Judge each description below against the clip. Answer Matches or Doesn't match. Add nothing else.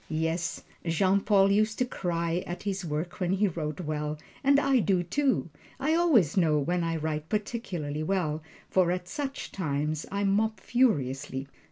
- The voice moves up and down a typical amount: Matches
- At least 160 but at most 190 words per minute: Matches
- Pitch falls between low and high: Matches